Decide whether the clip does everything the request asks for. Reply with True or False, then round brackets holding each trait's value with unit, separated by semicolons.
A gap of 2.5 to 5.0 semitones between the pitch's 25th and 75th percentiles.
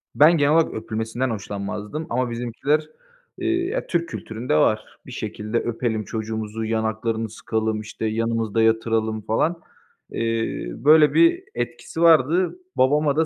False (5.5 semitones)